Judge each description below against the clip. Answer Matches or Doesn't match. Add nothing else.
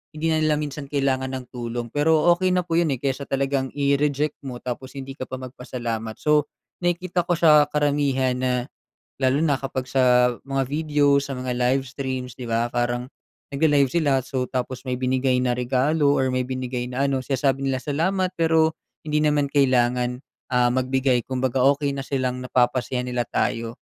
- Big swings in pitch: Doesn't match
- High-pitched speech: Doesn't match